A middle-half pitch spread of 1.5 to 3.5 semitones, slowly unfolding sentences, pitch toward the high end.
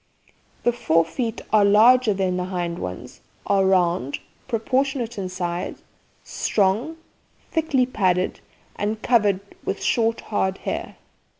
No: average, 4.5 semitones; slow, 120 wpm; high, 200 Hz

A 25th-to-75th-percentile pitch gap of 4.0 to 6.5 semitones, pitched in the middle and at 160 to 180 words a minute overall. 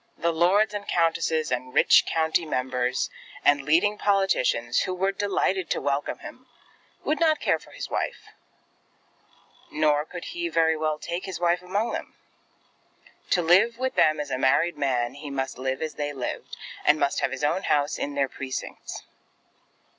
Yes: average, 5.3 semitones; medium, 160 Hz; average, 170 wpm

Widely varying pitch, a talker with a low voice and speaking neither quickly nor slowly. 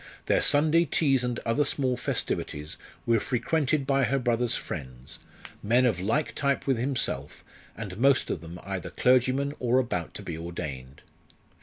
Yes: wide, 6.9 semitones; low, 125 Hz; average, 155 wpm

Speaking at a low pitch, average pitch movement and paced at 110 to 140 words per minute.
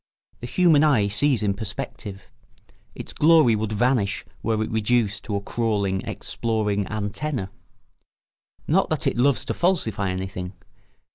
Yes: low, 110 Hz; average, 3.5 semitones; slow, 135 wpm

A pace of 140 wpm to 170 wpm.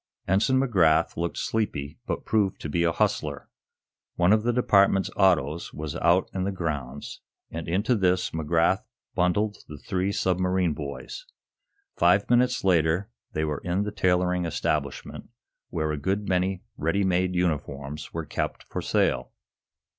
Yes: average, 145 wpm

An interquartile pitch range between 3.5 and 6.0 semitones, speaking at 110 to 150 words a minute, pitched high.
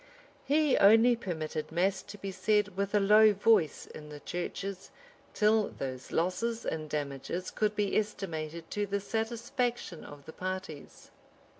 Yes: average, 5.1 semitones; average, 145 wpm; high, 195 Hz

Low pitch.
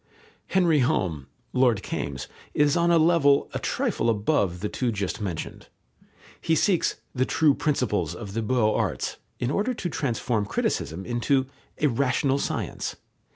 Yes: low, 125 Hz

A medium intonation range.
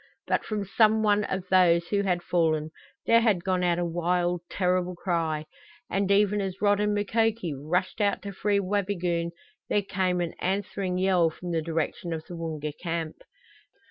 Yes: average, 3.0 semitones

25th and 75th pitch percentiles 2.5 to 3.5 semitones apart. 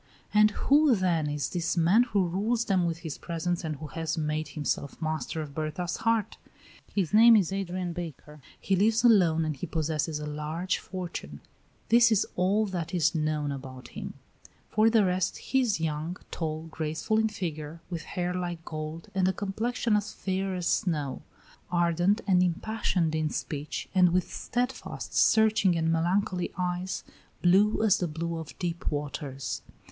No: average, 3.9 semitones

